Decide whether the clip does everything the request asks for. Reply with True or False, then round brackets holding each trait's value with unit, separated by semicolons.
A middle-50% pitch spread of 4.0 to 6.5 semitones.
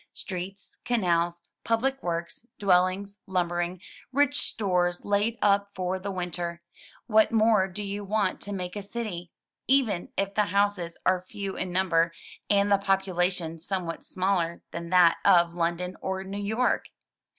False (2.4 semitones)